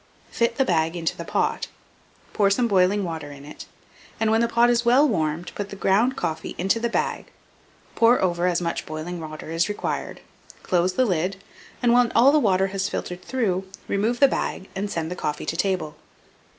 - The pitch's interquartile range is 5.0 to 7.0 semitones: Yes, wide, 5.4 semitones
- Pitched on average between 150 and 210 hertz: Yes, high, 190 Hz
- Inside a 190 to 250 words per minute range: Yes, average, 200 wpm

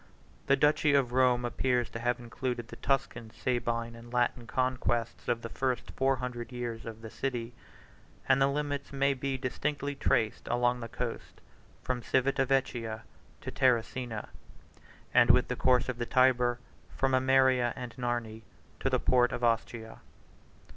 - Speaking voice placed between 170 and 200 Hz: No, low, 125 Hz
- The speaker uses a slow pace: No, average, 155 wpm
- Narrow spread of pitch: Yes, narrow, 1.9 semitones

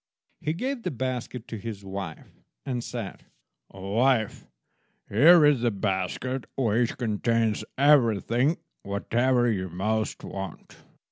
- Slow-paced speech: Yes, slow, 115 wpm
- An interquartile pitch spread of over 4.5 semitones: No, average, 4.2 semitones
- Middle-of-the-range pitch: No, low, 115 Hz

